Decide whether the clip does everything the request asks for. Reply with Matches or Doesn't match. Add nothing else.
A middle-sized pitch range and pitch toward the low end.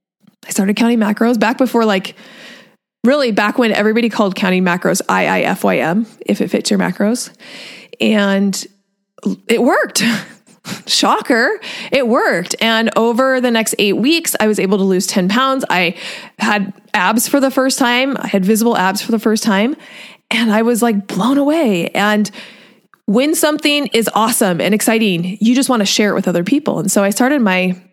Doesn't match